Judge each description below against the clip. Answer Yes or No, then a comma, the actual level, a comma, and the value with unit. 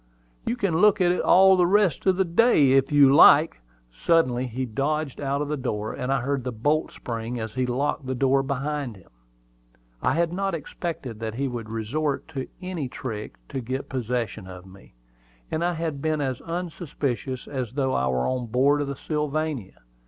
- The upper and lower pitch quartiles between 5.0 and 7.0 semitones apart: No, average, 4.2 semitones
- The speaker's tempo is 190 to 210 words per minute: Yes, average, 195 wpm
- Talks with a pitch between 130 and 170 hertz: Yes, low, 135 Hz